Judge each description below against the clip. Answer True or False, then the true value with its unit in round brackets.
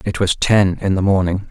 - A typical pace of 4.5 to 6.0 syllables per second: True (5.1 syllables/s)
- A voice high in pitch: False (95 Hz)